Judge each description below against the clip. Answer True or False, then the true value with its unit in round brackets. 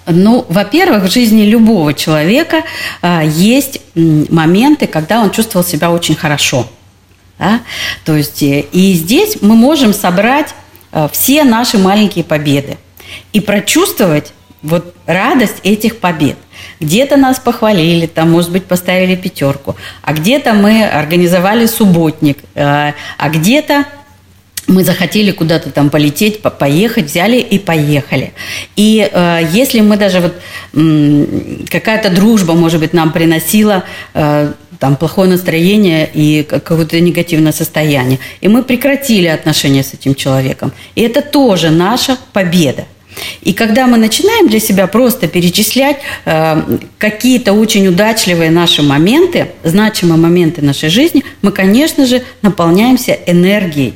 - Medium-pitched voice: True (180 Hz)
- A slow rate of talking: False (125 wpm)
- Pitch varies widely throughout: True (6.1 semitones)